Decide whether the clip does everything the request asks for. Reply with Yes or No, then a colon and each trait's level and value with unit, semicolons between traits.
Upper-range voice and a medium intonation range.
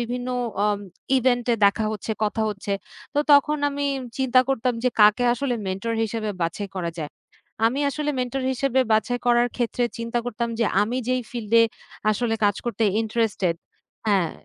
Yes: high, 235 Hz; average, 3.0 semitones